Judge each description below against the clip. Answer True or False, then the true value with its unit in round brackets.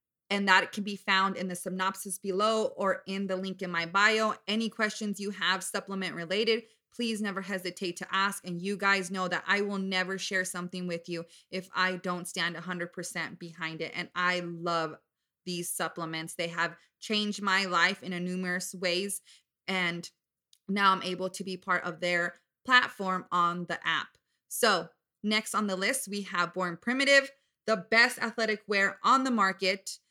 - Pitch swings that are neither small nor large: False (2.3 semitones)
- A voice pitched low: False (185 Hz)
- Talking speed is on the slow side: False (175 wpm)